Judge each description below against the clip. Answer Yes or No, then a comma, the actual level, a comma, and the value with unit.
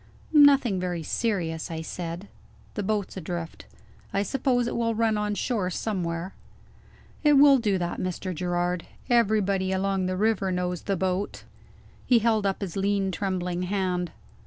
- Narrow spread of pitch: No, average, 3.3 semitones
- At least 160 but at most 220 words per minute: No, average, 150 wpm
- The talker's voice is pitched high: Yes, high, 195 Hz